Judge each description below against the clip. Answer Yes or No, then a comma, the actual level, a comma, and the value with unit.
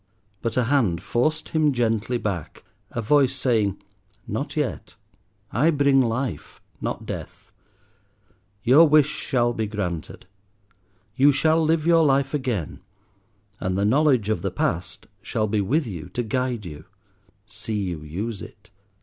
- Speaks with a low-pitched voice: Yes, low, 120 Hz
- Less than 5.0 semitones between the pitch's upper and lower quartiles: No, wide, 5.6 semitones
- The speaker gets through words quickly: No, average, 140 wpm